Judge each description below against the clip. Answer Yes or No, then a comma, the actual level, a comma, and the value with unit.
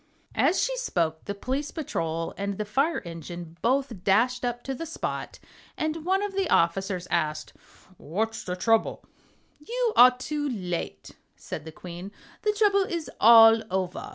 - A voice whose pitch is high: Yes, high, 225 Hz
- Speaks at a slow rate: No, average, 155 wpm